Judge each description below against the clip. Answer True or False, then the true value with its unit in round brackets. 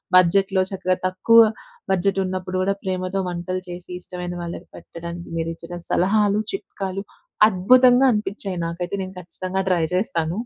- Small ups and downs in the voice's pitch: True (1.9 semitones)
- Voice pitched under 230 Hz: True (185 Hz)